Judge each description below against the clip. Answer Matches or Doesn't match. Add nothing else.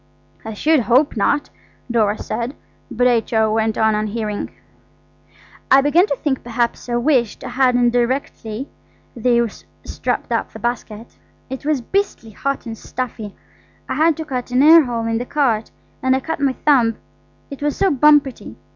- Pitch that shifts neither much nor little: Matches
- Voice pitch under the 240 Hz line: Doesn't match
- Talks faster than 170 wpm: Doesn't match